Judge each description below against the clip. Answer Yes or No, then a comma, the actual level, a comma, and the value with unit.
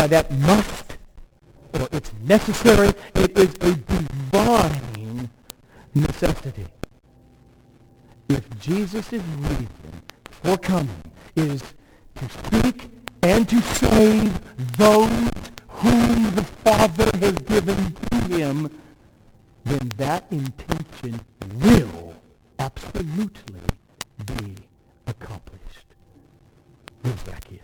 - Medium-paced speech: No, slow, 80 wpm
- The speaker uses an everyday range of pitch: No, wide, 8.9 semitones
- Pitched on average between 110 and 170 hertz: Yes, medium, 140 Hz